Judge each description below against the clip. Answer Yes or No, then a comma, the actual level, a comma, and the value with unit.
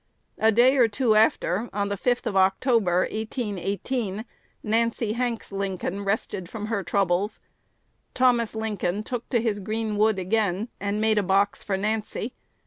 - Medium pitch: No, high, 215 Hz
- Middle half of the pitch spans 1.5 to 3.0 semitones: Yes, narrow, 2.5 semitones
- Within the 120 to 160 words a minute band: Yes, average, 150 wpm